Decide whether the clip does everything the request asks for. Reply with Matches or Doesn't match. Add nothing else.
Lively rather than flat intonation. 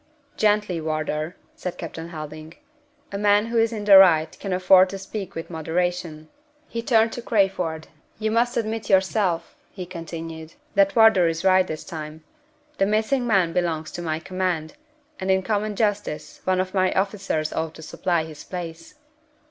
Doesn't match